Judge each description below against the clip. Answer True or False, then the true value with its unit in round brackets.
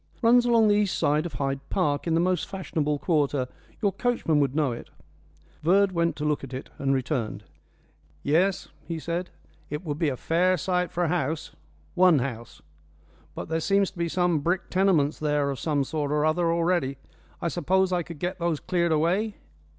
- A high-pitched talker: False (165 Hz)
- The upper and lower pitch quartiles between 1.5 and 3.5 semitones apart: False (3.9 semitones)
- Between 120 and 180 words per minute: False (190 wpm)